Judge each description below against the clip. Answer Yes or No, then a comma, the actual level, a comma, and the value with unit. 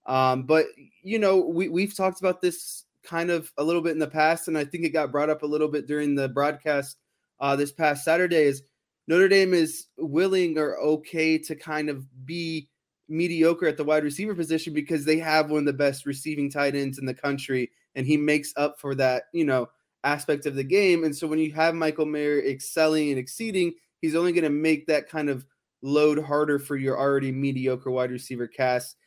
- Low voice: No, medium, 150 Hz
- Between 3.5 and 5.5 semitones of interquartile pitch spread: No, narrow, 2.6 semitones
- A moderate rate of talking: No, fast, 215 wpm